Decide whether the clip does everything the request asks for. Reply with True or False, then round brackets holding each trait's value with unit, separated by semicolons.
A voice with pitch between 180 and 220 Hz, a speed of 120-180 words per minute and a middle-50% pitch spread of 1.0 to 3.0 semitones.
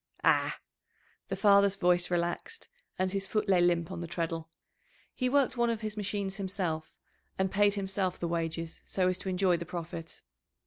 True (185 Hz; 175 wpm; 2.7 semitones)